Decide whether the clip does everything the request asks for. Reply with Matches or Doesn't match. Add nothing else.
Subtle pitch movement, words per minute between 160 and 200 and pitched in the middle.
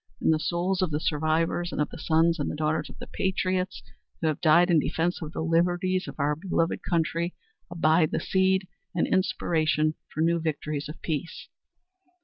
Matches